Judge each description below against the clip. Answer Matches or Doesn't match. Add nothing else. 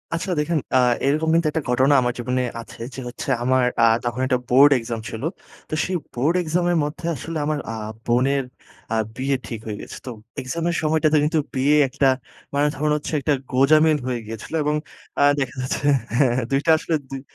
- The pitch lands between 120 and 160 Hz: Matches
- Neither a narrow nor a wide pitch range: Matches